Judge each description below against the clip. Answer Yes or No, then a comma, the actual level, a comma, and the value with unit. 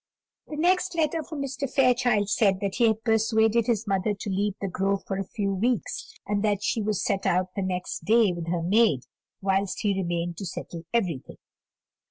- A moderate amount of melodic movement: Yes, average, 3.6 semitones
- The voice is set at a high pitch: Yes, high, 205 Hz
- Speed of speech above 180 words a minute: Yes, average, 200 wpm